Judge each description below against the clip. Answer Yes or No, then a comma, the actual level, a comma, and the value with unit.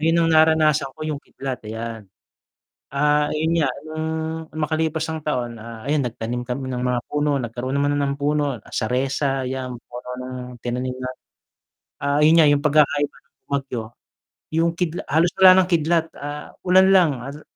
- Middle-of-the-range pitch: Yes, medium, 145 Hz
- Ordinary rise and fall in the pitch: Yes, average, 3.7 semitones